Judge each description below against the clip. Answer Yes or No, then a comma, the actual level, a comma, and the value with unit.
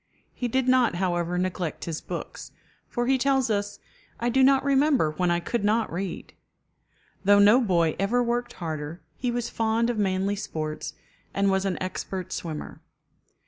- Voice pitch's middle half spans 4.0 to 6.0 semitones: Yes, average, 5.3 semitones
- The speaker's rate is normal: Yes, average, 165 wpm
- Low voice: No, high, 200 Hz